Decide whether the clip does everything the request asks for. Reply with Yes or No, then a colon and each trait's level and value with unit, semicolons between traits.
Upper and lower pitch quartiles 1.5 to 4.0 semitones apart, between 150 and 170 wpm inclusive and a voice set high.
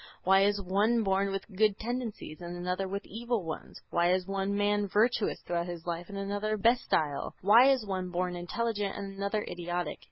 No: average, 3.0 semitones; average, 185 wpm; high, 195 Hz